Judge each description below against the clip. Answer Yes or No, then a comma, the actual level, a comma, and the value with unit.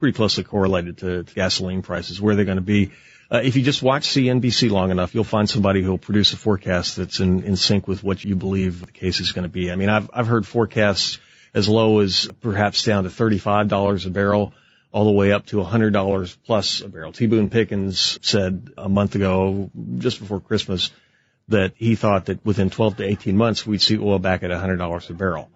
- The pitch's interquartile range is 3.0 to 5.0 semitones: No, narrow, 2.4 semitones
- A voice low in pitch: Yes, low, 100 Hz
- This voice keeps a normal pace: No, fast, 215 wpm